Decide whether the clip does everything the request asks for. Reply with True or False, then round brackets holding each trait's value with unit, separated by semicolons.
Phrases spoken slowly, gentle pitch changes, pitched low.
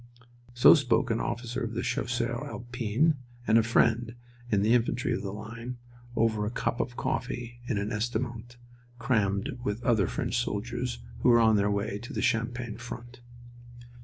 False (165 wpm; 1.9 semitones; 120 Hz)